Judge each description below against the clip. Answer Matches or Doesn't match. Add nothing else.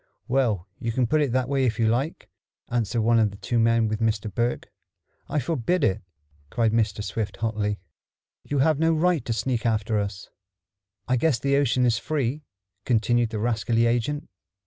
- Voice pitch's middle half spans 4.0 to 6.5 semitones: Doesn't match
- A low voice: Matches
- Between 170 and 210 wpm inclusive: Matches